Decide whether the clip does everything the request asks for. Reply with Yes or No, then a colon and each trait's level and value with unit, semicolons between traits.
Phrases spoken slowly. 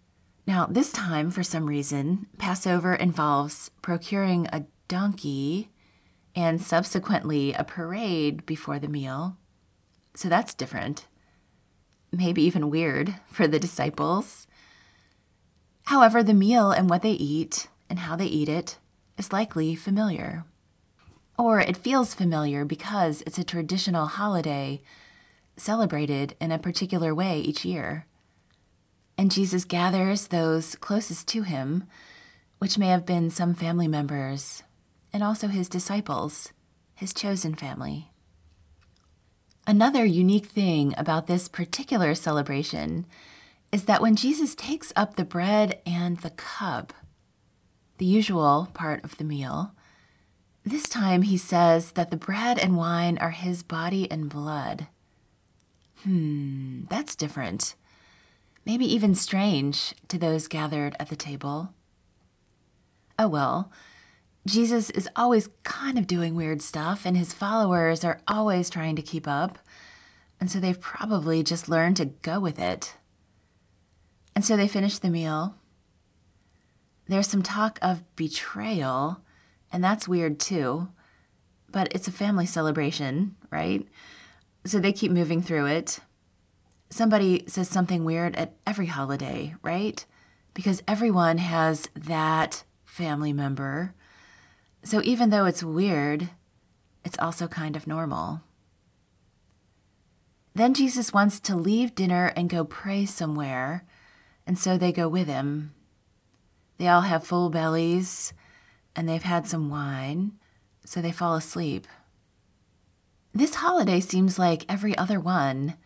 Yes: slow, 125 wpm